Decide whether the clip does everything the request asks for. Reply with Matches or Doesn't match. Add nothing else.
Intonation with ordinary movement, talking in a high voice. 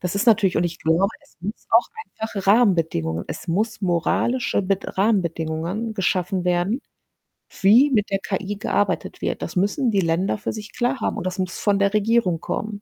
Matches